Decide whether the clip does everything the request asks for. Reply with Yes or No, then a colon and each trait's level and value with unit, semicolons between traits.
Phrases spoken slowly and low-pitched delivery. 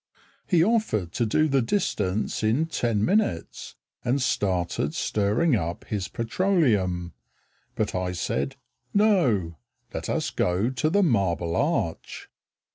Yes: slow, 120 wpm; low, 110 Hz